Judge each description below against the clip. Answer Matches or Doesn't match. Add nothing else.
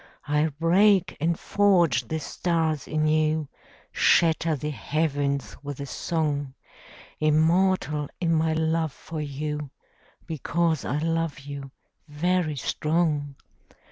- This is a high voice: Doesn't match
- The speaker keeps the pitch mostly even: Matches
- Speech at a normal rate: Doesn't match